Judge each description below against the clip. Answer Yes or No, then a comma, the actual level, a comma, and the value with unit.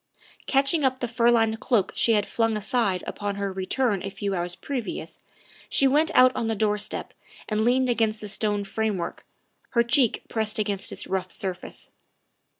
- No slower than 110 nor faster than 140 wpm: No, average, 170 wpm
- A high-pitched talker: Yes, high, 220 Hz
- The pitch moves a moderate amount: Yes, average, 3.4 semitones